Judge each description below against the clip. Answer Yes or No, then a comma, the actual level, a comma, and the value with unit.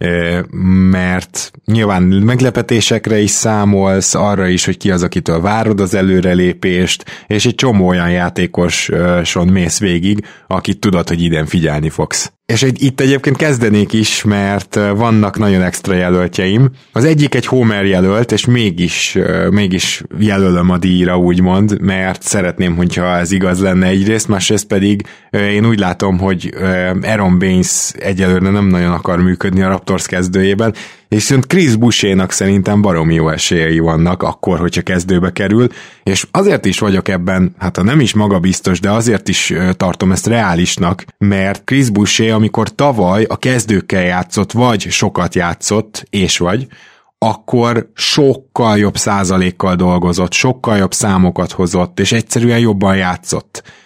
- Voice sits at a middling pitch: No, very low, 95 Hz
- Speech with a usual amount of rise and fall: Yes, average, 3.1 semitones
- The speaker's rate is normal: Yes, average, 140 wpm